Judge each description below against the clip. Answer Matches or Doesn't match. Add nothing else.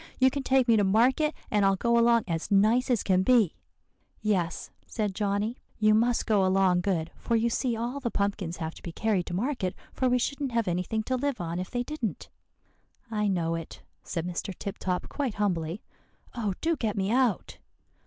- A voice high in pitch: Matches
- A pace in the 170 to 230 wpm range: Matches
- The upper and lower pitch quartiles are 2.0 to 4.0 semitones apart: Doesn't match